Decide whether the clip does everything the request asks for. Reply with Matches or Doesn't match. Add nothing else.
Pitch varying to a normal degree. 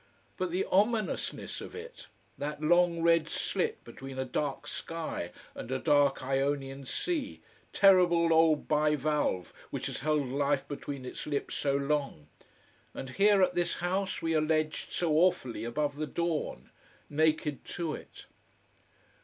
Matches